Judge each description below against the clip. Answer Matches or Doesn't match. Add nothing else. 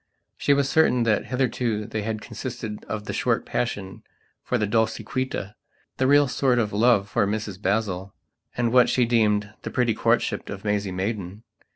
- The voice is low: Matches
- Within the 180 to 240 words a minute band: Doesn't match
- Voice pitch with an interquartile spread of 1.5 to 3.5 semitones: Matches